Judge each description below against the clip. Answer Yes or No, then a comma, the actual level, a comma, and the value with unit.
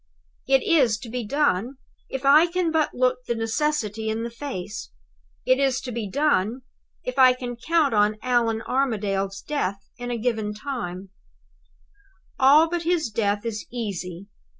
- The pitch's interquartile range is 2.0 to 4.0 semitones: No, average, 4.6 semitones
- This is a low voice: No, high, 245 Hz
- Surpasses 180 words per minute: No, average, 155 wpm